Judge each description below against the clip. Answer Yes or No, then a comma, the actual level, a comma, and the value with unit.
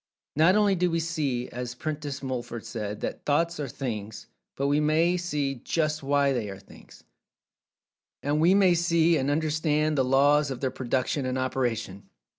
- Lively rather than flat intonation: No, average, 3.8 semitones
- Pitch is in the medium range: Yes, medium, 145 Hz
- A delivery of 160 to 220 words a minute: Yes, average, 170 wpm